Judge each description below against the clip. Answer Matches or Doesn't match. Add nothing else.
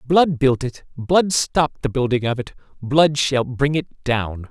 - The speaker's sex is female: Doesn't match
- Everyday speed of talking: Matches